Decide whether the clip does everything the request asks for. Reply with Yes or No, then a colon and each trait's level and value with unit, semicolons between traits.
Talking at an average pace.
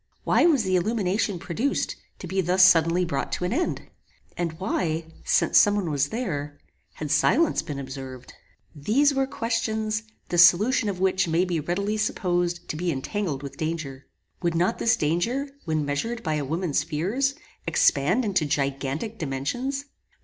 Yes: average, 160 wpm